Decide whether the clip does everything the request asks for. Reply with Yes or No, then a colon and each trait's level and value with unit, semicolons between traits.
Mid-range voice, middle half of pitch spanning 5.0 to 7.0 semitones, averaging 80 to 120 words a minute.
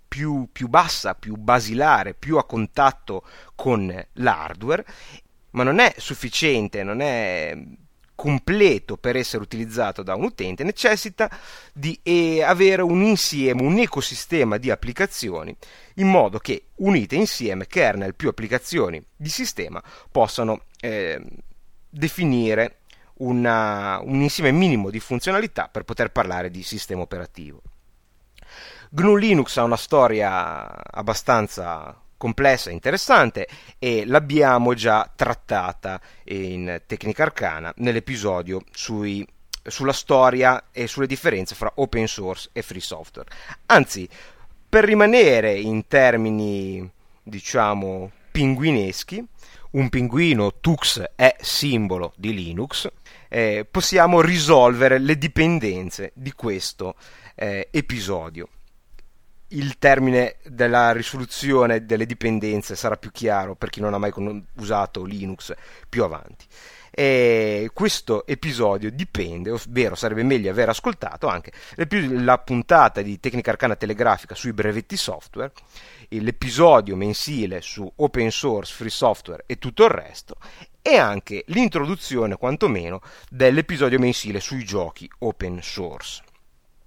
No: low, 120 Hz; wide, 5.4 semitones; slow, 115 wpm